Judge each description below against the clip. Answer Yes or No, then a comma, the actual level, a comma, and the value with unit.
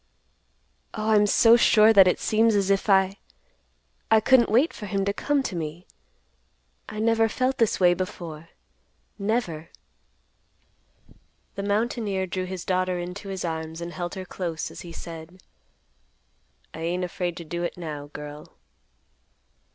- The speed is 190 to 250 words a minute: No, average, 145 wpm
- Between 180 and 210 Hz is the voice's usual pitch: Yes, medium, 185 Hz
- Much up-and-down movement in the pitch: No, average, 4.1 semitones